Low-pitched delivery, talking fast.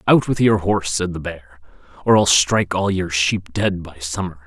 Yes: very low, 90 Hz; fast, 215 wpm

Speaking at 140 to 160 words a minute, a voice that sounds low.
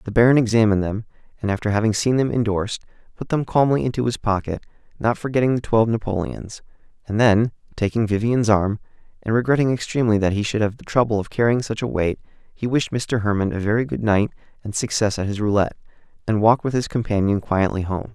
No: average, 200 wpm; low, 110 Hz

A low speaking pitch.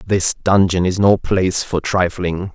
Yes: very low, 95 Hz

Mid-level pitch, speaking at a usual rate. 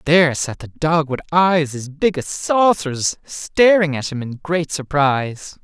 Yes: medium, 155 Hz; average, 170 wpm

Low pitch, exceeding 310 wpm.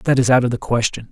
Yes: low, 120 Hz; fast, 325 wpm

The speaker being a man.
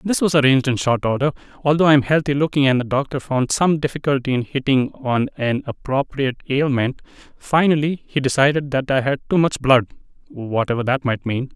Yes: male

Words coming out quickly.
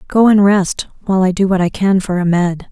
Yes: fast, 245 wpm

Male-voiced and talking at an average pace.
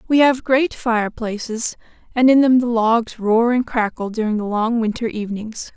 No: female; average, 175 wpm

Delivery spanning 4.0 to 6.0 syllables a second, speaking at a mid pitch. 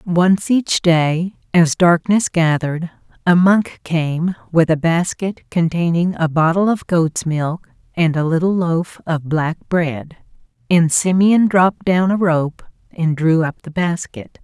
No: 3.8 syllables/s; medium, 170 Hz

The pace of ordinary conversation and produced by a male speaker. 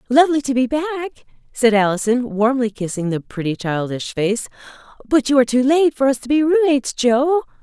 No: average, 180 wpm; female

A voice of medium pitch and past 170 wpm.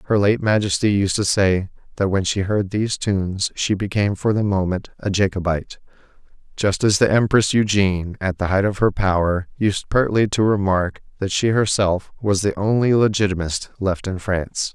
No: low, 100 Hz; average, 180 wpm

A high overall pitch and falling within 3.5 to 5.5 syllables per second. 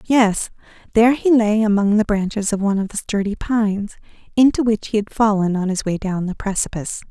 No: high, 210 Hz; 5.8 syllables/s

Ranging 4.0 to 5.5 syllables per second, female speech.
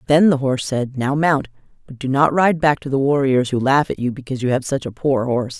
No: 5.9 syllables/s; female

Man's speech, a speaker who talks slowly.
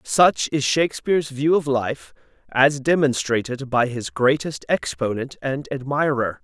Yes: male; slow, 130 wpm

